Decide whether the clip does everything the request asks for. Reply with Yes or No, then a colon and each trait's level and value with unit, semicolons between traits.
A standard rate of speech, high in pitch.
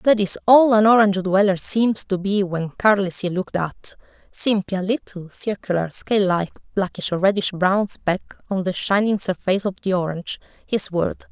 Yes: average, 175 wpm; high, 195 Hz